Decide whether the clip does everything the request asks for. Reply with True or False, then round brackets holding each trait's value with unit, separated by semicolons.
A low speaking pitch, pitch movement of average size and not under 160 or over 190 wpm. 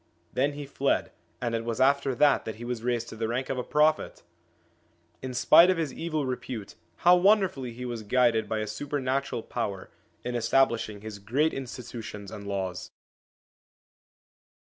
True (125 Hz; 3.9 semitones; 165 wpm)